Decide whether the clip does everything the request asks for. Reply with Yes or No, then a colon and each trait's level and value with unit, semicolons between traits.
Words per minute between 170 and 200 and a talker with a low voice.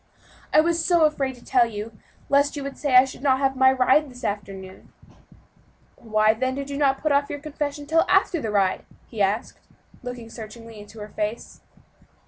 No: average, 190 wpm; very high, 260 Hz